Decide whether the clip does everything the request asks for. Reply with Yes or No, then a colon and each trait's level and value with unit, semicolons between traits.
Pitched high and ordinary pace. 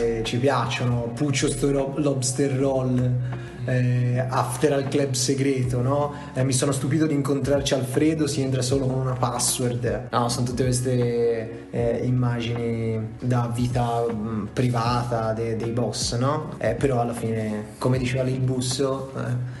No: low, 125 Hz; average, 145 wpm